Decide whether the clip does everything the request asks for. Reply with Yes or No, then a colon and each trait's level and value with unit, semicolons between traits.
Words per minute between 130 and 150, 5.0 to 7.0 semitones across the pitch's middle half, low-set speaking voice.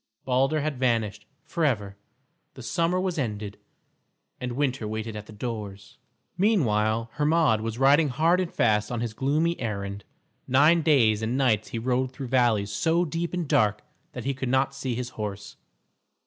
No: average, 160 wpm; wide, 5.4 semitones; low, 125 Hz